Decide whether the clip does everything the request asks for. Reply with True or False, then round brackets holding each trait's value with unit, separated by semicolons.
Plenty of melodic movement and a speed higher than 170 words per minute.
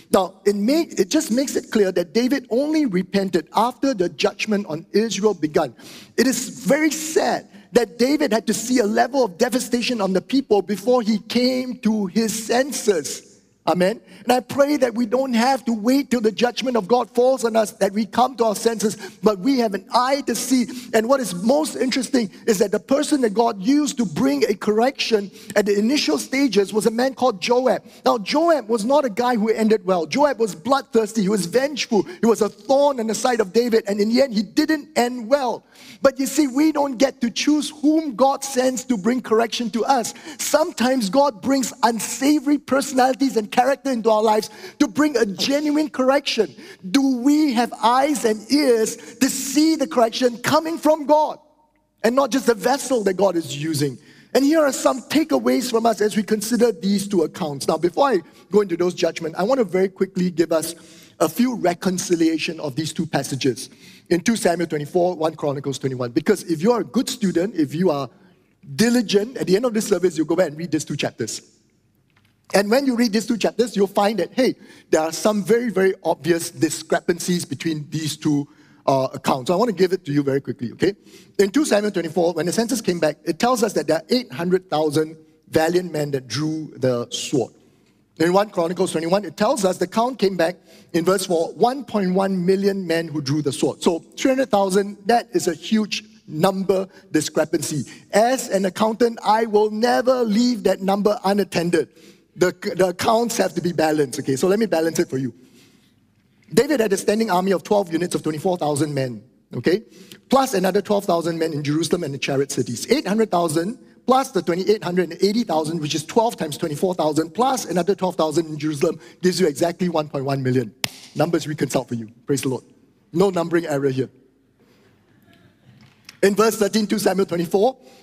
True (6.4 semitones; 195 wpm)